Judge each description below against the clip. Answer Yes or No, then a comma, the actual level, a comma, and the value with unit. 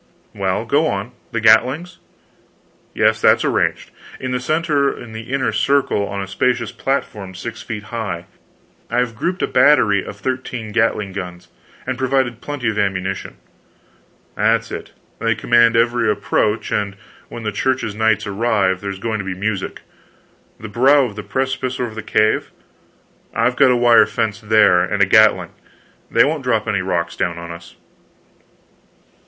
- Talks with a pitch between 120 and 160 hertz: No, low, 110 Hz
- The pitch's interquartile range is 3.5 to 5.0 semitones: Yes, average, 4.1 semitones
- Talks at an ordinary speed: Yes, average, 160 wpm